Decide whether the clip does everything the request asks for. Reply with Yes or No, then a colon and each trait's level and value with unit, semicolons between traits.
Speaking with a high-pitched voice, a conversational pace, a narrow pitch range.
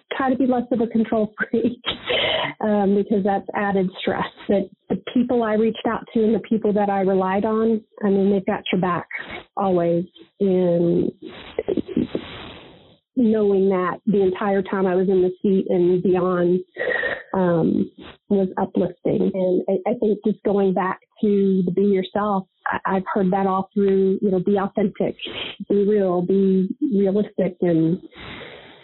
Yes: high, 200 Hz; average, 150 wpm; narrow, 2.1 semitones